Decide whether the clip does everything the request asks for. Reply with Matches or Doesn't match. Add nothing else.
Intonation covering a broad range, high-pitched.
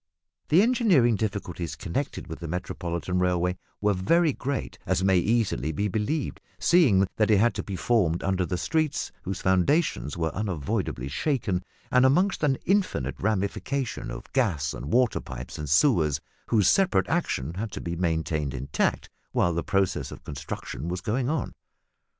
Doesn't match